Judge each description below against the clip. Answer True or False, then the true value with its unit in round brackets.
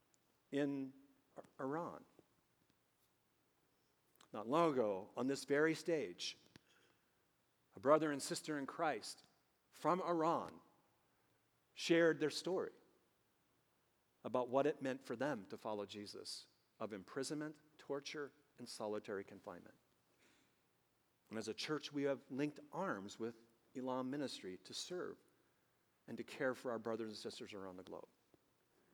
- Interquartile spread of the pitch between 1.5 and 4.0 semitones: False (5.0 semitones)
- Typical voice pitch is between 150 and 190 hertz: False (135 Hz)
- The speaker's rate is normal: False (120 wpm)